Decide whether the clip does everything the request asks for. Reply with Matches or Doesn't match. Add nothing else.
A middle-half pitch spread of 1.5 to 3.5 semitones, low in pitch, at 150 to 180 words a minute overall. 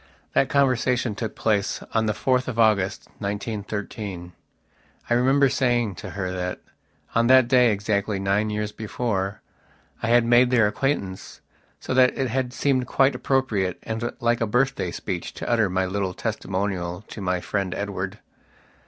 Doesn't match